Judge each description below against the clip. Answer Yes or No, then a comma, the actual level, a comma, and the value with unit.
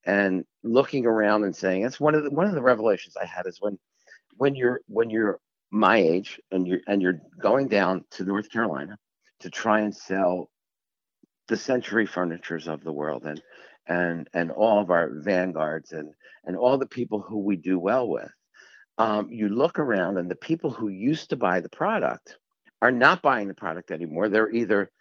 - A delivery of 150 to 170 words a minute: No, average, 190 wpm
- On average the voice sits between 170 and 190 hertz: No, low, 105 Hz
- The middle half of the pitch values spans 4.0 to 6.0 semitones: Yes, average, 4.4 semitones